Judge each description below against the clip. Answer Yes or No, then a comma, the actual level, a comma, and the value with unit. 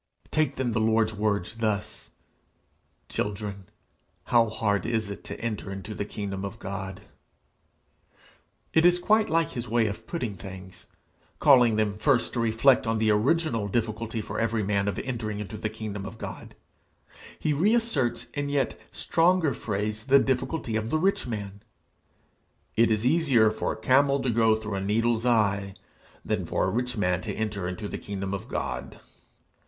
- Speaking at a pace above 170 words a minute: No, average, 165 wpm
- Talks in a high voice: No, low, 110 Hz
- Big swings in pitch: No, average, 3.6 semitones